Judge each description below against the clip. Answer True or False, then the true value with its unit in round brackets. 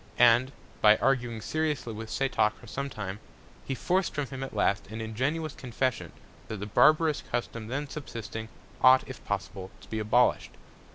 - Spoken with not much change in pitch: False (3.9 semitones)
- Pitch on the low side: True (120 Hz)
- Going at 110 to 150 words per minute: False (165 wpm)